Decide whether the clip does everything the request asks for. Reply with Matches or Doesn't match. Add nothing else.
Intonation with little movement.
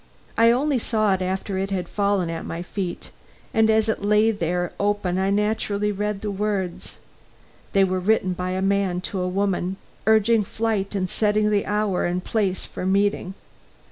Matches